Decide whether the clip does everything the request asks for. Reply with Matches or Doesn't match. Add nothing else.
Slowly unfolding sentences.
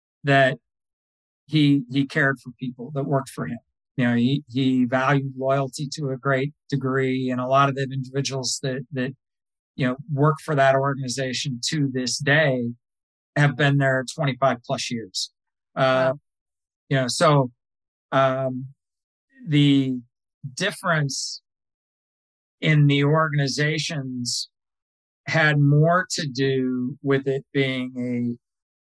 Matches